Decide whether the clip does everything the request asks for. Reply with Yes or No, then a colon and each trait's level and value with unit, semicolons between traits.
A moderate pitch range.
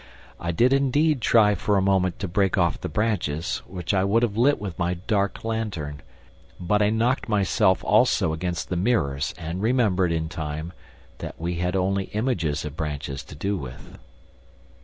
Yes: average, 4.4 semitones